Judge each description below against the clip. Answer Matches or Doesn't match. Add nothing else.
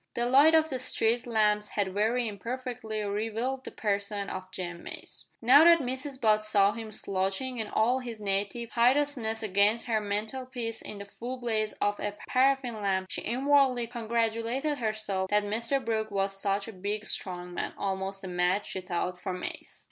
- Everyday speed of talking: Matches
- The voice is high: Matches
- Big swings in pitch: Doesn't match